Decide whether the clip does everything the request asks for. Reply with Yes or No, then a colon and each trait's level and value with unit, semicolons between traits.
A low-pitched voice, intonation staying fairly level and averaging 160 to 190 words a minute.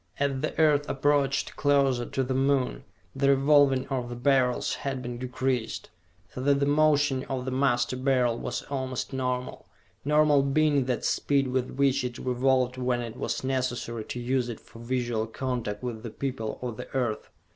Yes: low, 130 Hz; narrow, 2.0 semitones; average, 175 wpm